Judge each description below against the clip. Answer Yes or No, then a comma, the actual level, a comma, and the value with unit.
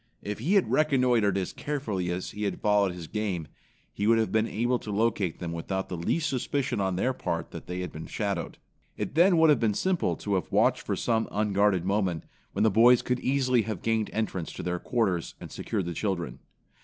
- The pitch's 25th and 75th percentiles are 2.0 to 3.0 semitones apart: No, average, 4.7 semitones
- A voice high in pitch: No, low, 105 Hz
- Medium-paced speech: No, fast, 215 wpm